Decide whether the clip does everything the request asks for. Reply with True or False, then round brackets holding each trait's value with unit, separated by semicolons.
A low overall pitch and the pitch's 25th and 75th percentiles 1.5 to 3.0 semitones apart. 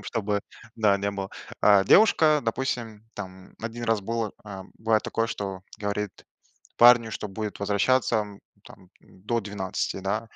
True (105 Hz; 2.5 semitones)